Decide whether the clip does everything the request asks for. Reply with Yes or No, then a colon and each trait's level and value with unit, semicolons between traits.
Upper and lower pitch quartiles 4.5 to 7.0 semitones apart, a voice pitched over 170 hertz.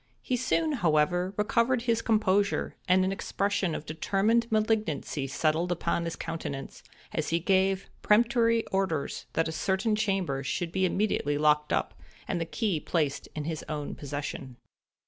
Yes: wide, 5.6 semitones; medium, 185 Hz